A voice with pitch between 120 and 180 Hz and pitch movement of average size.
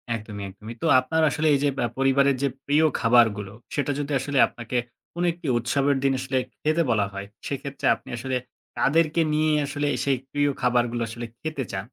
Yes: low, 135 Hz; average, 3.6 semitones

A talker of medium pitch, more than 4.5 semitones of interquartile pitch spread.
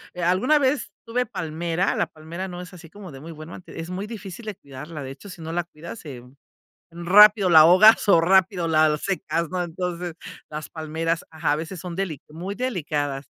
No: medium, 170 Hz; average, 3.4 semitones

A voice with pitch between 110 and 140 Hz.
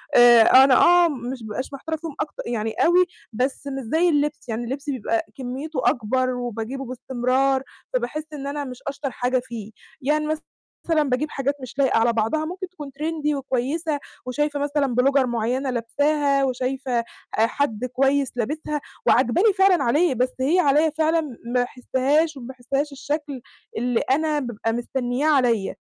No: very high, 270 Hz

